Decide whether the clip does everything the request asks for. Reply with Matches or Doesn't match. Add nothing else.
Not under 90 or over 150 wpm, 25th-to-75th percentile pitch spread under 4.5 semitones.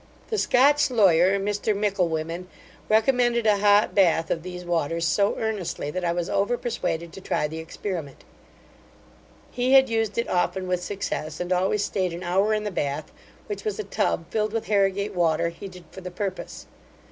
Doesn't match